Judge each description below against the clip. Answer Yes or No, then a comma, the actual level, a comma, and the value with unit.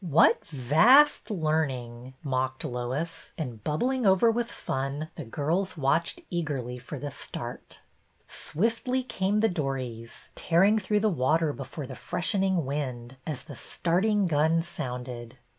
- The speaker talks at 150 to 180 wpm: No, average, 140 wpm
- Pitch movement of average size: No, wide, 6.5 semitones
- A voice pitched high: No, medium, 155 Hz